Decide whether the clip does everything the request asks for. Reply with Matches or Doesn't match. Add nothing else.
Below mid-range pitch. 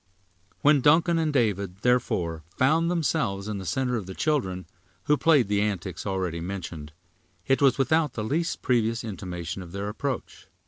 Matches